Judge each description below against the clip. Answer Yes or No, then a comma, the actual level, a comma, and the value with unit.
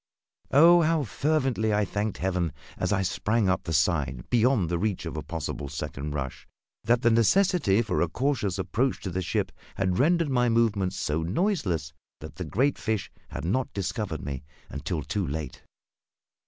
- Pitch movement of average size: No, wide, 6.7 semitones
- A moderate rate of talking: Yes, average, 170 wpm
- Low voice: Yes, low, 100 Hz